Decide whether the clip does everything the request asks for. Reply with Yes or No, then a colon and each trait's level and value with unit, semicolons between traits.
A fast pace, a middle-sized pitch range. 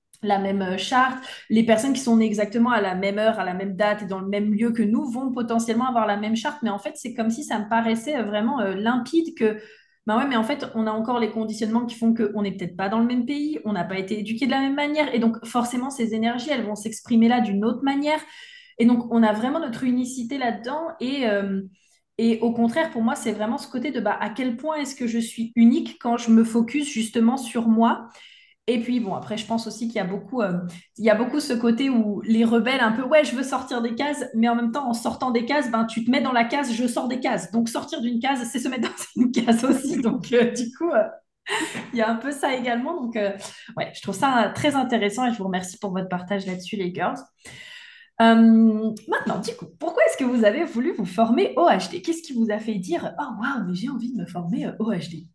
Yes: fast, 255 wpm; average, 3.3 semitones